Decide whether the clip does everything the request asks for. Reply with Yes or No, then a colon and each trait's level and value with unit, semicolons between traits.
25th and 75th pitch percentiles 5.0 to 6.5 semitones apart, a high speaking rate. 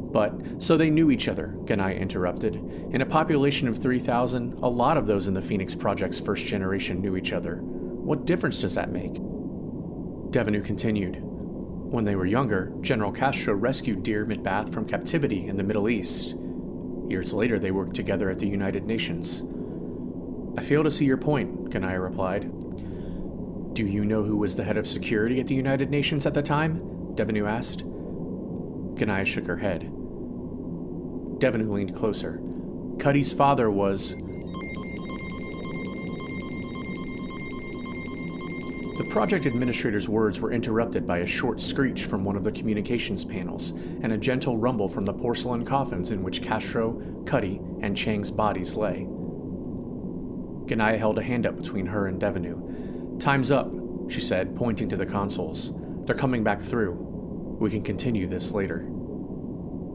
No: wide, 5.6 semitones; average, 150 wpm